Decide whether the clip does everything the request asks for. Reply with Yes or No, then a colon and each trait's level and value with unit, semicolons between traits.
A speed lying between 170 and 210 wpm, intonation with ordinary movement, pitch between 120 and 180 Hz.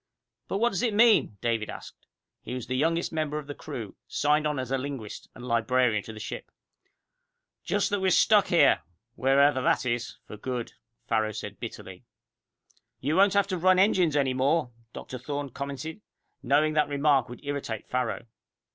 Yes: average, 175 wpm; average, 4.4 semitones; medium, 140 Hz